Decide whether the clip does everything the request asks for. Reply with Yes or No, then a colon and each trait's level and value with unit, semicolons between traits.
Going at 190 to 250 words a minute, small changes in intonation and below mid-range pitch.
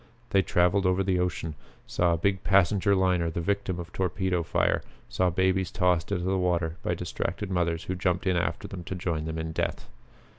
Yes: average, 195 wpm; narrow, 1.9 semitones; very low, 90 Hz